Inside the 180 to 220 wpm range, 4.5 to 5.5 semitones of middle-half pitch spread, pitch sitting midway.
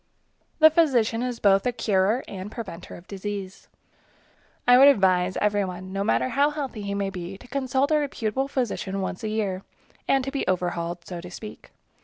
No: average, 185 wpm; average, 5.2 semitones; high, 205 Hz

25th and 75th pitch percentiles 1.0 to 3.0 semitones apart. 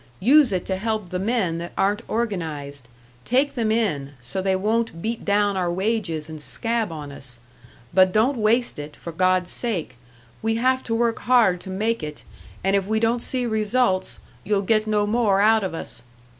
No: average, 4.3 semitones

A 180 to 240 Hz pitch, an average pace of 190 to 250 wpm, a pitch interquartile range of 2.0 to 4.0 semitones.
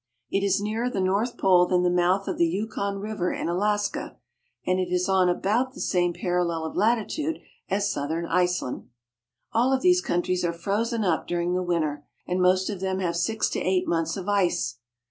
Yes: medium, 185 Hz; average, 200 wpm; average, 2.8 semitones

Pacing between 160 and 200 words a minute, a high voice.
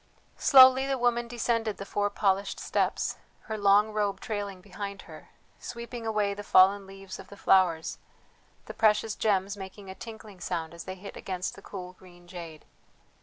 Yes: average, 170 wpm; high, 200 Hz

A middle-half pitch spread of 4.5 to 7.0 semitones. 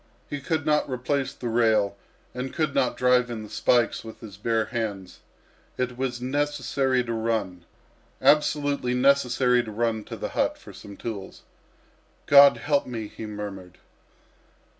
No: average, 3.8 semitones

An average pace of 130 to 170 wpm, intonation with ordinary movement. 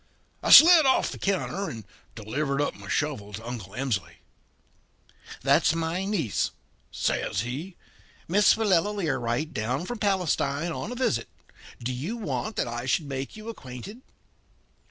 No: average, 145 wpm; wide, 8.2 semitones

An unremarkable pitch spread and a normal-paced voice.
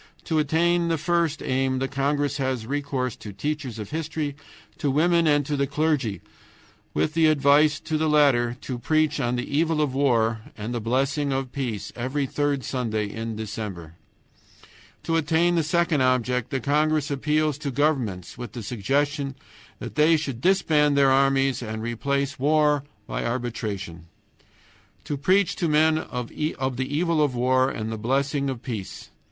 Yes: average, 3.7 semitones; average, 165 wpm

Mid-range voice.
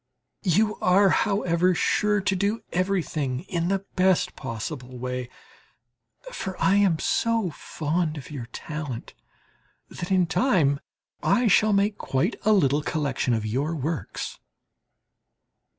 Yes: medium, 170 Hz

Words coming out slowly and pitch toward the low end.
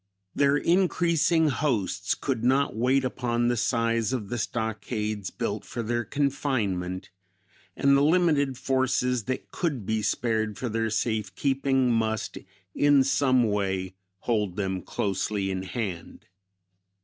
Yes: slow, 130 wpm; low, 120 Hz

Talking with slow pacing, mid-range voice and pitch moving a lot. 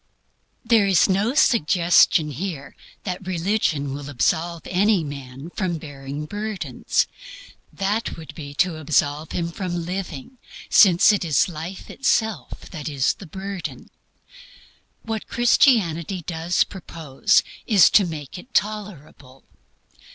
No: slow, 120 wpm; medium, 175 Hz; average, 4.7 semitones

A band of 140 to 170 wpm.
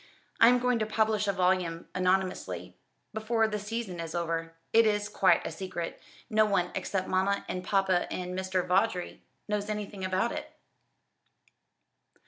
Yes: average, 150 wpm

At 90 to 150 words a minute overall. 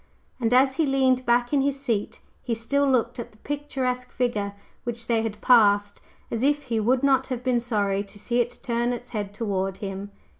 No: average, 200 wpm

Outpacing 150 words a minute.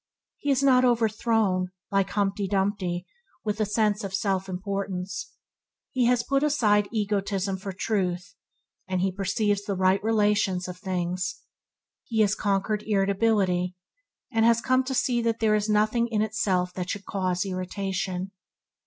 No: average, 145 wpm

